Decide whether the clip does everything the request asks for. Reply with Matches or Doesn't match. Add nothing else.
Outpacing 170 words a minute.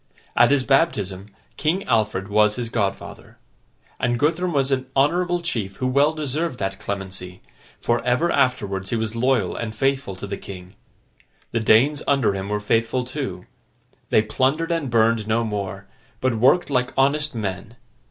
Doesn't match